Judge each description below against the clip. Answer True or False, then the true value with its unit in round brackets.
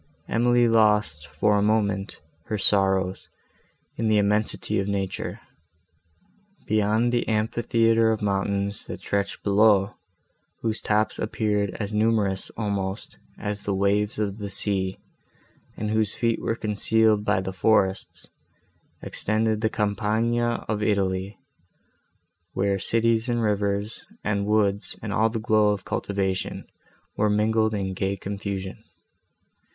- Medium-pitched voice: False (105 Hz)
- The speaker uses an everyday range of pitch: False (1.8 semitones)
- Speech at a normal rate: False (125 wpm)